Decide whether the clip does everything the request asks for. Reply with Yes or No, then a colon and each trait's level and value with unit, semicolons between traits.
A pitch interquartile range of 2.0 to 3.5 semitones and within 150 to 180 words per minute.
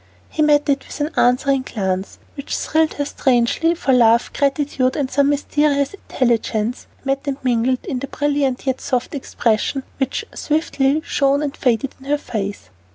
Yes: average, 2.7 semitones; average, 160 wpm